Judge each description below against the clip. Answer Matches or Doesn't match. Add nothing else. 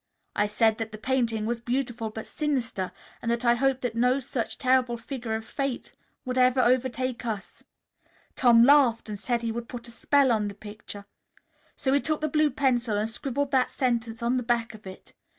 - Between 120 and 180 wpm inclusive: Doesn't match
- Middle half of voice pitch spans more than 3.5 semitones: Doesn't match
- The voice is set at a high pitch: Matches